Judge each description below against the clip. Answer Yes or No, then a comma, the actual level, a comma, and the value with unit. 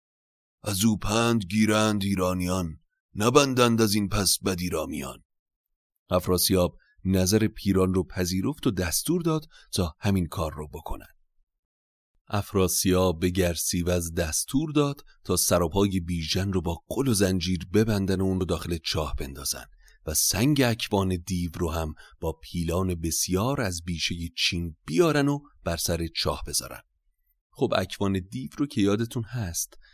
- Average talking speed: Yes, average, 140 wpm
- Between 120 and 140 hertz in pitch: No, very low, 95 Hz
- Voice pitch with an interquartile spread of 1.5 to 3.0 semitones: No, average, 3.8 semitones